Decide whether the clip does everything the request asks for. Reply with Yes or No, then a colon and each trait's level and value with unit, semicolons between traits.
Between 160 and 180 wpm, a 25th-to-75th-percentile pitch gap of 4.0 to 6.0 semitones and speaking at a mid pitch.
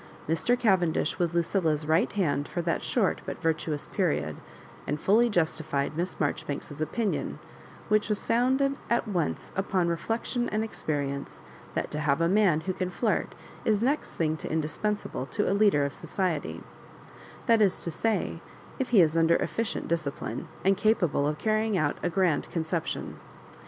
Yes: average, 165 wpm; wide, 5.4 semitones; medium, 175 Hz